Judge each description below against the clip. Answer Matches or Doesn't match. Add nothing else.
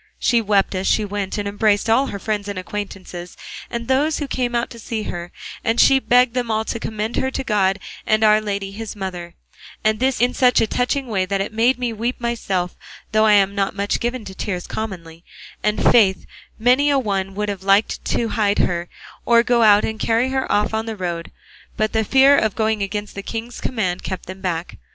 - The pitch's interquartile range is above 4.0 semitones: Doesn't match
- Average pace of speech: Doesn't match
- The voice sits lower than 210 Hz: Doesn't match